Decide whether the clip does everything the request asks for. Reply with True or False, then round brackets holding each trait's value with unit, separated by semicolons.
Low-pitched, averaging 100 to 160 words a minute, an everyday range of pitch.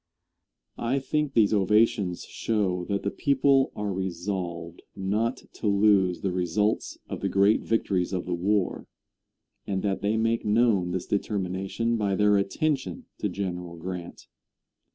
True (100 Hz; 140 wpm; 3.3 semitones)